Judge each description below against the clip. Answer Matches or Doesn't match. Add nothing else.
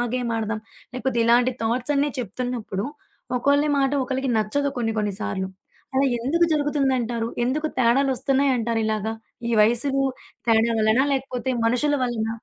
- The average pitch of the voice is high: Matches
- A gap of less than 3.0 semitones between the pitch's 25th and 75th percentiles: Doesn't match